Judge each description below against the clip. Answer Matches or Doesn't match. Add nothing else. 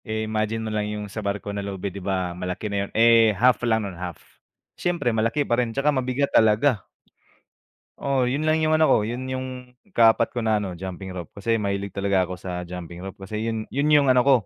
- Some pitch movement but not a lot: Matches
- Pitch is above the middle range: Doesn't match